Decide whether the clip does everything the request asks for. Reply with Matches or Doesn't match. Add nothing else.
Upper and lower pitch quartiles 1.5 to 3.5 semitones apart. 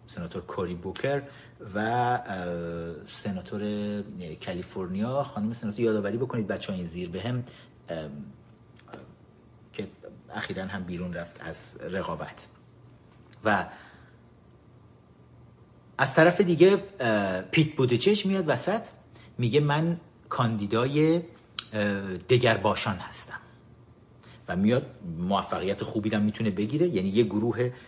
Doesn't match